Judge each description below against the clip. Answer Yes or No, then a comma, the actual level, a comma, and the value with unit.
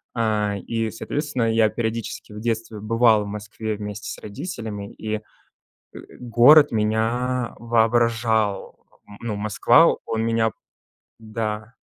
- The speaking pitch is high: No, low, 110 Hz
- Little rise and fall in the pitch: Yes, narrow, 1.6 semitones